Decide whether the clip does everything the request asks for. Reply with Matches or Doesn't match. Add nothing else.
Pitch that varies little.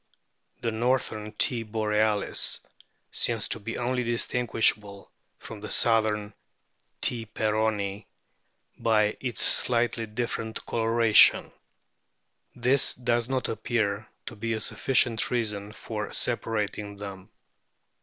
Matches